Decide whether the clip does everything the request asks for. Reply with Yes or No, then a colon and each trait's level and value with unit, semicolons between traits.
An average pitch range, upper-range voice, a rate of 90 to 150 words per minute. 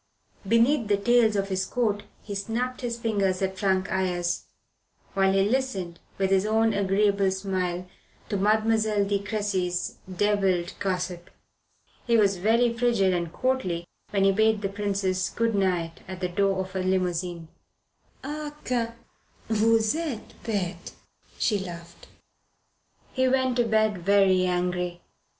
Yes: average, 3.2 semitones; high, 200 Hz; average, 140 wpm